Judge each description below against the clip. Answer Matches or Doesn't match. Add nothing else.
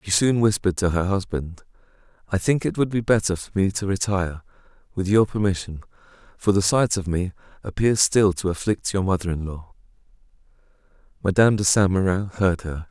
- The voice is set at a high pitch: Doesn't match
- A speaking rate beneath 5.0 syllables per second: Doesn't match